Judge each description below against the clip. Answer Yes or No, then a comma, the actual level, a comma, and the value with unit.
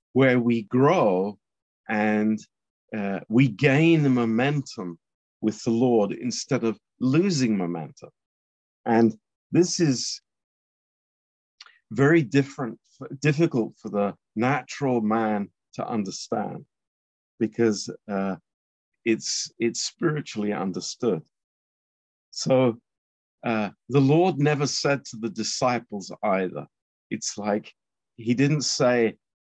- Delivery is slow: Yes, slow, 100 wpm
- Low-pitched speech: Yes, low, 115 Hz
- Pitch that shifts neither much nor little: Yes, average, 4.9 semitones